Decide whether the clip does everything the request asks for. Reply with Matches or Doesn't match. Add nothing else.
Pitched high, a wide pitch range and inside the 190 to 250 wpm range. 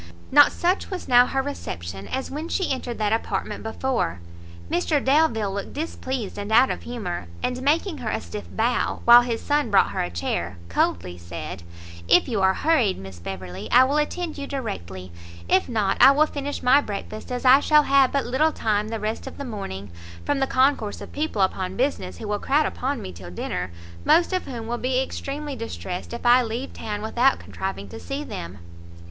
Matches